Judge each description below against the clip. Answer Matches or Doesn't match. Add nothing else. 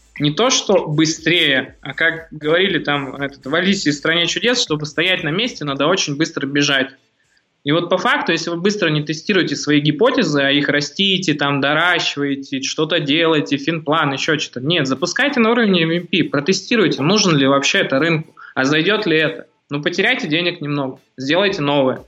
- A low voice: Doesn't match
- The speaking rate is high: Matches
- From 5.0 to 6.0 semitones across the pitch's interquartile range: Doesn't match